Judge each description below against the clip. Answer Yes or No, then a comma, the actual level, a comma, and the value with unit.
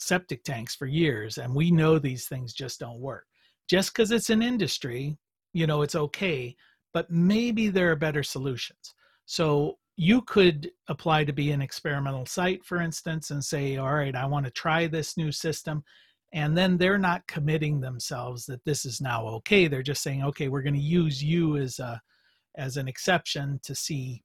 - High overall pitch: No, medium, 150 Hz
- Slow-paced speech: No, average, 190 wpm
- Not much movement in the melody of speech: No, average, 3.8 semitones